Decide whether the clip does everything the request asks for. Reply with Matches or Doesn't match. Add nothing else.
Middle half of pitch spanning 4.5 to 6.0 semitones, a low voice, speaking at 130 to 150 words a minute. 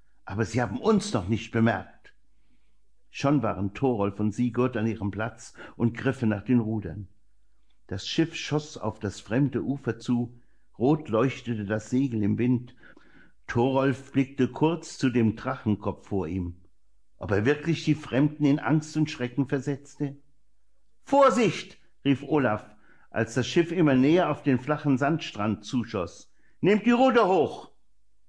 Matches